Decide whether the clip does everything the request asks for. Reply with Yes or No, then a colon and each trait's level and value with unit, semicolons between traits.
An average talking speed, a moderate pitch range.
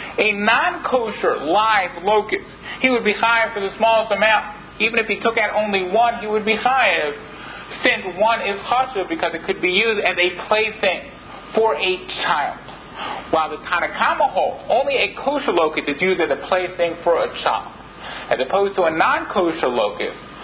Yes: average, 180 wpm; average, 3.4 semitones